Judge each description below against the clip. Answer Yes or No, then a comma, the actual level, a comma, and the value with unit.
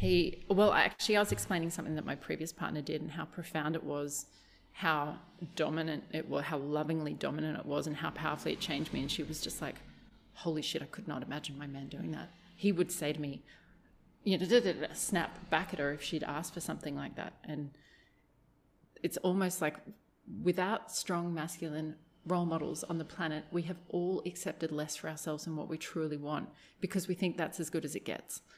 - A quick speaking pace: Yes, fast, 215 wpm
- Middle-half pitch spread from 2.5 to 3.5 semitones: Yes, average, 2.8 semitones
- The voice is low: No, medium, 160 Hz